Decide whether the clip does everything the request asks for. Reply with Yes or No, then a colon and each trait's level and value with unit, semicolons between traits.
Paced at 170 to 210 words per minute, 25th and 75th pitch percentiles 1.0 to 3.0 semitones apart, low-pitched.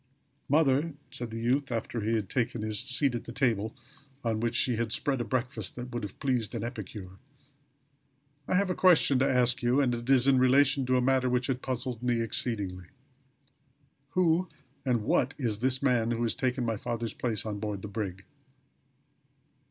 Yes: average, 190 wpm; average, 2.7 semitones; low, 120 Hz